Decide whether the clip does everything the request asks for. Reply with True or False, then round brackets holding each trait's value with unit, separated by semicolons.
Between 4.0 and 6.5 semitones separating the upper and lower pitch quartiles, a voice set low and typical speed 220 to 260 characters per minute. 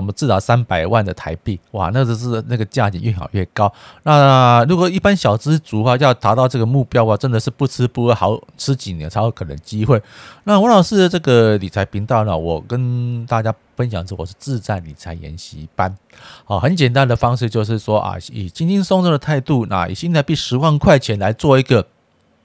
False (5.1 semitones; 115 Hz; 315 characters per minute)